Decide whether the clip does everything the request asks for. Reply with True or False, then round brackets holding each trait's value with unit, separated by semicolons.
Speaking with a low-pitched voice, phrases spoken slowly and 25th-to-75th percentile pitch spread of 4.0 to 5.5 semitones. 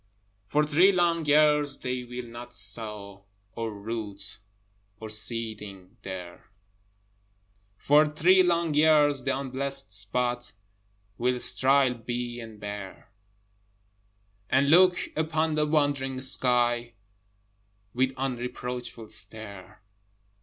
True (125 Hz; 100 wpm; 5.0 semitones)